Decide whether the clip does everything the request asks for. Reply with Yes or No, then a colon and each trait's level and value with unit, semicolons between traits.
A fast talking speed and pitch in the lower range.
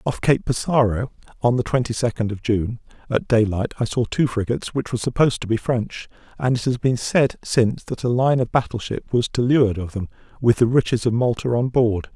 Yes: fast, 225 wpm; low, 120 Hz